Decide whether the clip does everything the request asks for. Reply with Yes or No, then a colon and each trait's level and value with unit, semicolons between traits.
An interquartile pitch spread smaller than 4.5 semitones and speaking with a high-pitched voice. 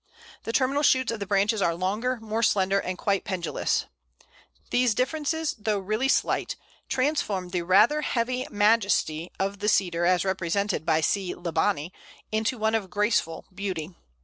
Yes: average, 3.9 semitones; high, 205 Hz